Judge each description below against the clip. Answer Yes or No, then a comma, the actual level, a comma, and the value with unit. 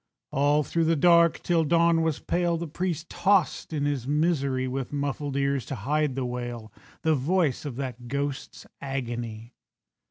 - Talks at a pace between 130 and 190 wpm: Yes, average, 160 wpm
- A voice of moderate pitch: Yes, medium, 145 Hz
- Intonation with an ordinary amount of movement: Yes, average, 4.0 semitones